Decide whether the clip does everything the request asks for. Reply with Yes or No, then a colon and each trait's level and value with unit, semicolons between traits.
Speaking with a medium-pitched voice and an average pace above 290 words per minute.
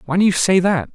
Yes: medium, 175 Hz; fast, 320 wpm